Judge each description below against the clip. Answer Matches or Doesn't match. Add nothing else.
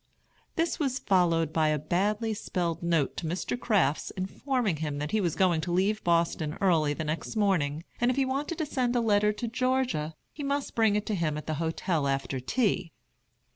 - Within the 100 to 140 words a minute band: Doesn't match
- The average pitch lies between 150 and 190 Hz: Matches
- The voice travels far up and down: Matches